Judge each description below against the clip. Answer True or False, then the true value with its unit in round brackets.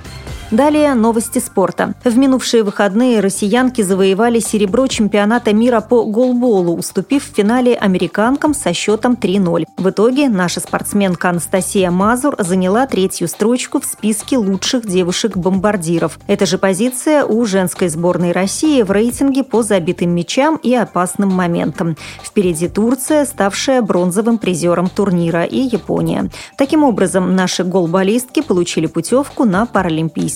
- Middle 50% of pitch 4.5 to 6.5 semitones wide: True (5.0 semitones)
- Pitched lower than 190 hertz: False (205 Hz)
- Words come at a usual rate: True (125 wpm)